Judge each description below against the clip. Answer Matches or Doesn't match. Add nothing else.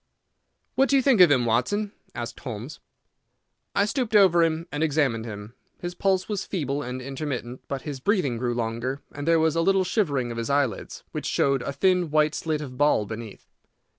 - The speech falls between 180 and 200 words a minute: Matches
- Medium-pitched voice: Matches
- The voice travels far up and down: Matches